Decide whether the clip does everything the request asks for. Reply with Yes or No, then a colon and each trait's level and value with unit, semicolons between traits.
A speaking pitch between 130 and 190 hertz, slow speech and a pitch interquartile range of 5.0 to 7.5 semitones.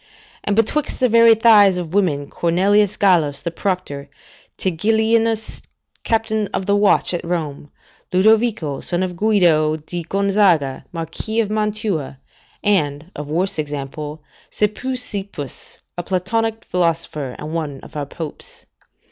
Yes: medium, 185 Hz; slow, 125 wpm; wide, 5.5 semitones